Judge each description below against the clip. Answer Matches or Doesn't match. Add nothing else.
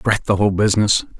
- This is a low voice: Matches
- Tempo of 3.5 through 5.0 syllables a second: Doesn't match